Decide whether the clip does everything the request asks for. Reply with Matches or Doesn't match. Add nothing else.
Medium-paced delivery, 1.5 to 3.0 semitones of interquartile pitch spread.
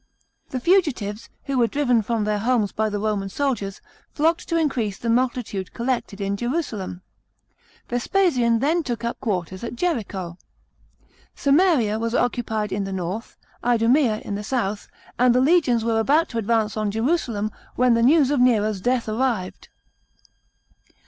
Doesn't match